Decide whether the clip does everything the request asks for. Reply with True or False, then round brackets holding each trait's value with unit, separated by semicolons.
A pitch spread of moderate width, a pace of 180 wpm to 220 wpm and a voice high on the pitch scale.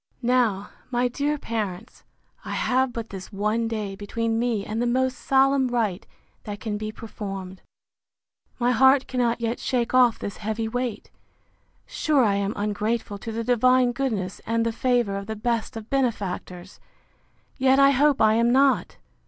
False (3.2 semitones; 160 wpm; 230 Hz)